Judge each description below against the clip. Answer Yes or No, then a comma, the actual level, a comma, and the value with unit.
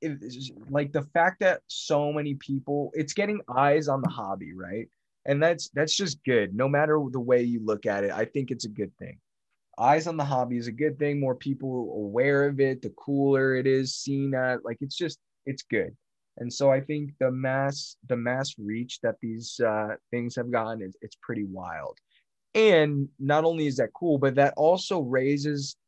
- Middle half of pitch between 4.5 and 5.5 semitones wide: No, average, 3.1 semitones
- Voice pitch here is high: No, low, 135 Hz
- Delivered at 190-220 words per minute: Yes, fast, 205 wpm